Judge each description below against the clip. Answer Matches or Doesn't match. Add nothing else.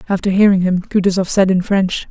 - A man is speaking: Doesn't match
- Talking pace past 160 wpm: Matches